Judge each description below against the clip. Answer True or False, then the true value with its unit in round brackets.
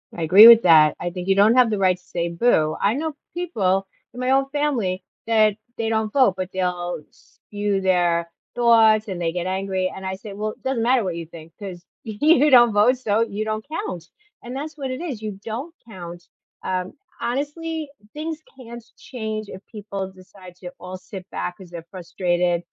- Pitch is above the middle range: True (205 Hz)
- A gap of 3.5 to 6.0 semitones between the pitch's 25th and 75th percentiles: True (4.8 semitones)